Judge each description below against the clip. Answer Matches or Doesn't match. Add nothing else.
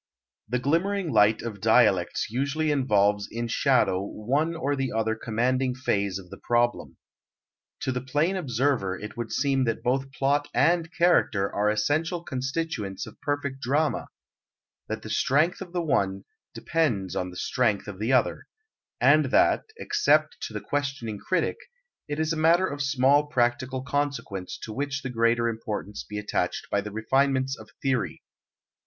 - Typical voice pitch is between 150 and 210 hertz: Doesn't match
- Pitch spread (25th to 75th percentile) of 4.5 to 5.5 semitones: Matches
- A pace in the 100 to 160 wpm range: Matches